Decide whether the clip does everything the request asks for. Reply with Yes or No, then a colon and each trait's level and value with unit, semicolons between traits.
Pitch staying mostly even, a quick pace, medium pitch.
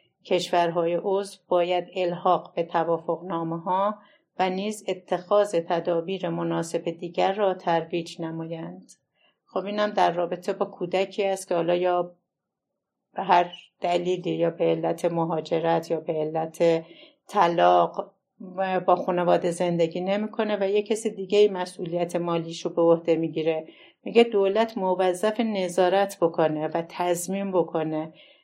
No: narrow, 2.3 semitones; average, 130 wpm; medium, 175 Hz